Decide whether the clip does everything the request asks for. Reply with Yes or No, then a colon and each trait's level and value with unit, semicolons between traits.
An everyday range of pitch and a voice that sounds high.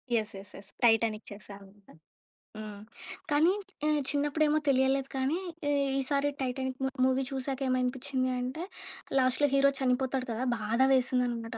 Yes: average, 3.1 semitones; very high, 255 Hz